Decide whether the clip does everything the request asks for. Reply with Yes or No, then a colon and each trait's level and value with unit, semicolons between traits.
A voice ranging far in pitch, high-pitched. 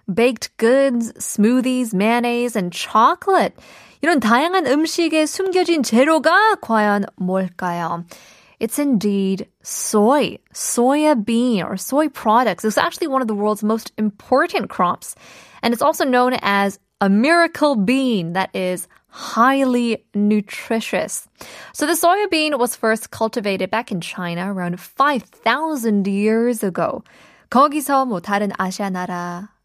Yes: wide, 6.0 semitones; high, 230 Hz